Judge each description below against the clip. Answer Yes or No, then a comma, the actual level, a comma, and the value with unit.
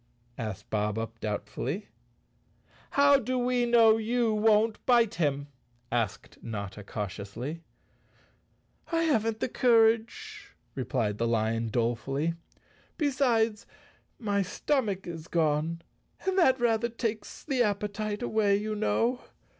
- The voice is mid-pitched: No, high, 210 Hz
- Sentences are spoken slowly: Yes, slow, 115 wpm